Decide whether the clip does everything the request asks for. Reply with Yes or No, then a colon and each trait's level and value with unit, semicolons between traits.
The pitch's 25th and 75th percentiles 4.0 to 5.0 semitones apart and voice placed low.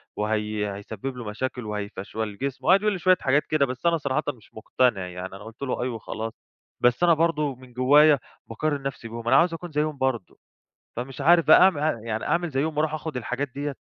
No: wide, 5.4 semitones; low, 130 Hz